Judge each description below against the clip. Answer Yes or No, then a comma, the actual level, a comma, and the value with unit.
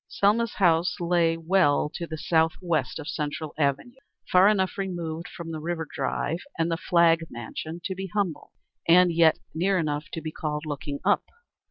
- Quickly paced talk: No, average, 175 wpm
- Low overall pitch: No, medium, 165 Hz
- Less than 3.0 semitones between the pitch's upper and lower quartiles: Yes, narrow, 2.4 semitones